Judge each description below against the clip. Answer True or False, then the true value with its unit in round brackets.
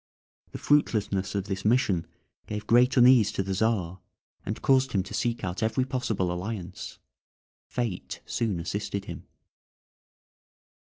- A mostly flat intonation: False (4.1 semitones)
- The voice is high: False (105 Hz)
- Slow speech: True (130 wpm)